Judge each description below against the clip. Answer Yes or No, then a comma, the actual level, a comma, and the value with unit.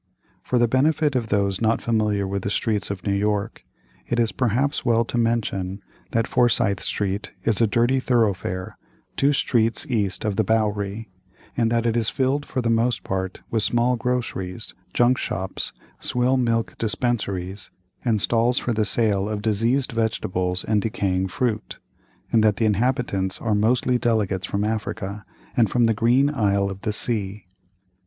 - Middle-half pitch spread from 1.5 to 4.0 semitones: Yes, average, 3.1 semitones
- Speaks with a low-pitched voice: Yes, low, 110 Hz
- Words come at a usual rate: Yes, average, 165 wpm